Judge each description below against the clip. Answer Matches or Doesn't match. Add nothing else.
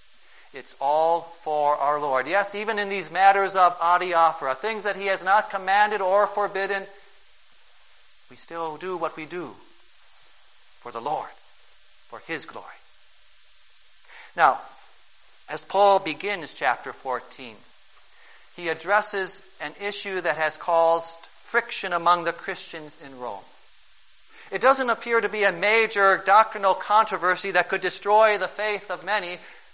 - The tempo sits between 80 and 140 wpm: Matches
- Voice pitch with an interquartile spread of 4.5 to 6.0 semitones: Doesn't match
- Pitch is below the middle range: Doesn't match